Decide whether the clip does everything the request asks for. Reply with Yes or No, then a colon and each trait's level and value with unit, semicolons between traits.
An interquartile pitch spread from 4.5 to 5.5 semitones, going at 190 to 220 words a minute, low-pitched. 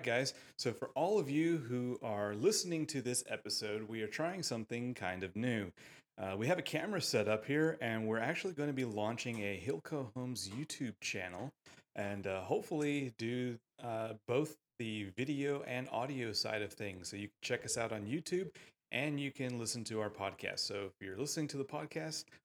Yes: average, 5.1 semitones; average, 200 wpm; low, 120 Hz